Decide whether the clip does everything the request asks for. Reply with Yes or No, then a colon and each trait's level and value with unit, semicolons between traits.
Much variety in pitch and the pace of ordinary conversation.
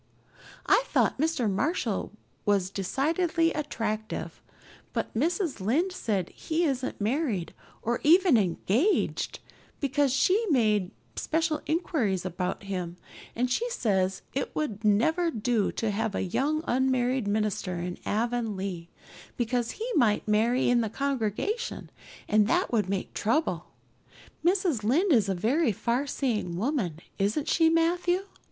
No: wide, 7.3 semitones; slow, 130 wpm